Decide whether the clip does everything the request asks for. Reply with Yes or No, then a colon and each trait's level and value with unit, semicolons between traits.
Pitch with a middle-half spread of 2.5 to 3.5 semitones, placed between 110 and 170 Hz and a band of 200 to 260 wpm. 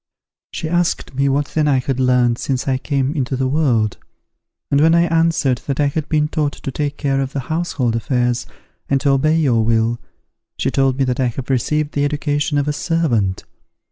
Yes: average, 2.9 semitones; medium, 140 Hz; fast, 205 wpm